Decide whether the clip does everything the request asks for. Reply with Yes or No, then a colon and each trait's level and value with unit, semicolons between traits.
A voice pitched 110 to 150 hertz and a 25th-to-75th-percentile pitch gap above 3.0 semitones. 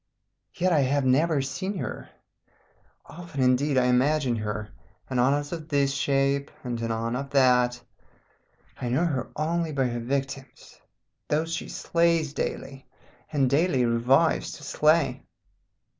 Yes: medium, 140 Hz; average, 3.6 semitones